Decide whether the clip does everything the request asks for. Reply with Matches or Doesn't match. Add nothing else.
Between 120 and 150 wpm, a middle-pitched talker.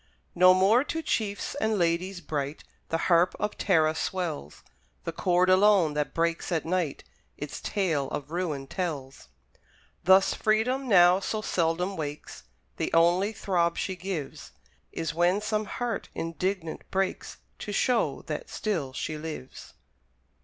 Matches